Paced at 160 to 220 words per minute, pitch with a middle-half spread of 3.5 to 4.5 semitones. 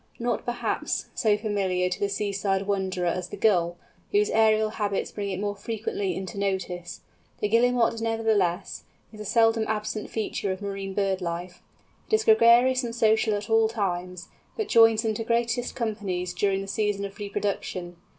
No: average, 170 wpm; average, 2.9 semitones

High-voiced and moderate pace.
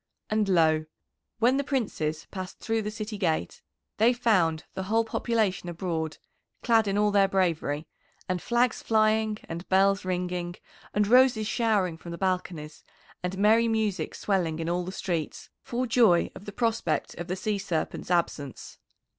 Yes: high, 195 Hz; average, 160 wpm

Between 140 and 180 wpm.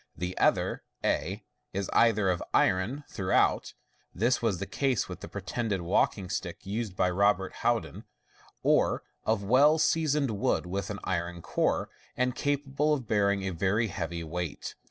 Yes: average, 160 wpm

